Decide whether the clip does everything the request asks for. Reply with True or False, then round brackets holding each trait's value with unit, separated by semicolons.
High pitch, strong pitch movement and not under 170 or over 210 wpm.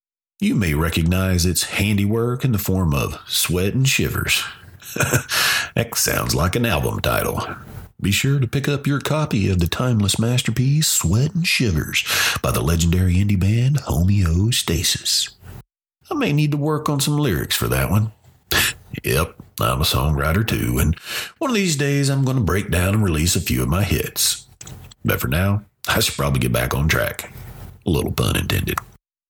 False (105 Hz; 6.8 semitones; 175 wpm)